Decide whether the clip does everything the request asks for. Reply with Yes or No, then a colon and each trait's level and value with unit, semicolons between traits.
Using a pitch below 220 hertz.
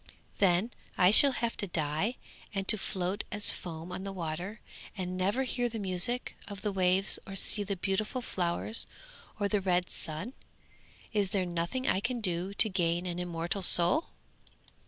Yes: high, 190 Hz